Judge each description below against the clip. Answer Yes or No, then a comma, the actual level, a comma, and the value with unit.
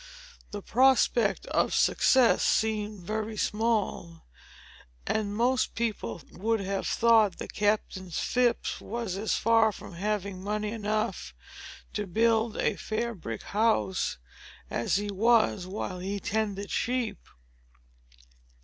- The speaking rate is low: Yes, slow, 115 wpm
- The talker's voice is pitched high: Yes, high, 210 Hz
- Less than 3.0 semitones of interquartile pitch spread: Yes, narrow, 2.5 semitones